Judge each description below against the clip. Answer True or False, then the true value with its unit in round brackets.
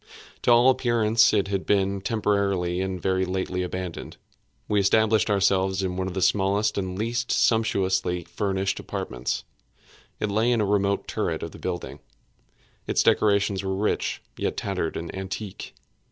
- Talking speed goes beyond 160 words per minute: False (155 wpm)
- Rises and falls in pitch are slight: True (2.1 semitones)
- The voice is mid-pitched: False (100 Hz)